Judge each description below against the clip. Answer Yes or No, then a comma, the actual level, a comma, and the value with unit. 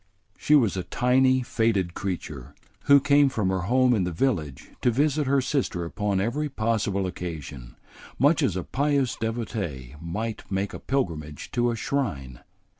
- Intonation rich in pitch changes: Yes, wide, 6.9 semitones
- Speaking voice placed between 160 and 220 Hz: No, low, 110 Hz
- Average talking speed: Yes, average, 160 wpm